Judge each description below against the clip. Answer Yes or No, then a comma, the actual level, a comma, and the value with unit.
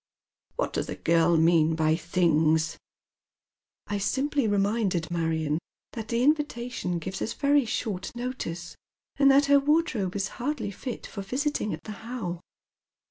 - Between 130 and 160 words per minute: Yes, average, 155 wpm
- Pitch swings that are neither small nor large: No, wide, 7.1 semitones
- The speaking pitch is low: No, high, 205 Hz